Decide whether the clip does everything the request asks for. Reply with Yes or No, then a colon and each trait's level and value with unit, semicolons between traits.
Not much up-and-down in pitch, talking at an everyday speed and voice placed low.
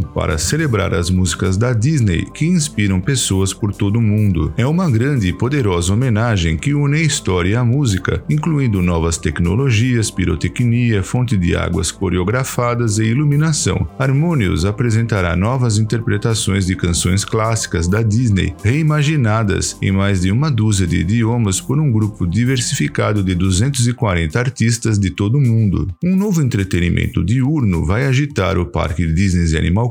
No: average, 5.0 semitones; average, 145 wpm; low, 105 Hz